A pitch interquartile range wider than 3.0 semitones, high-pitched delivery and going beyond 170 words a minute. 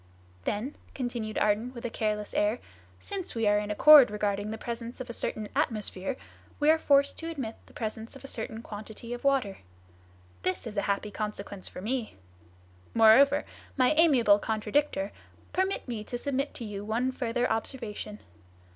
No: average, 4.0 semitones; high, 230 Hz; average, 165 wpm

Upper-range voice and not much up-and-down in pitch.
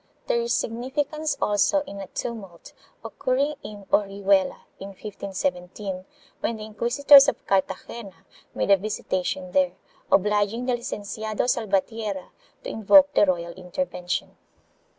No: high, 210 Hz; average, 4.1 semitones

